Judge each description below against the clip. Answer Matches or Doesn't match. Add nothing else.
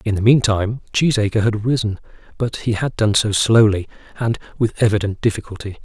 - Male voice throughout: Matches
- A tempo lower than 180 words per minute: Matches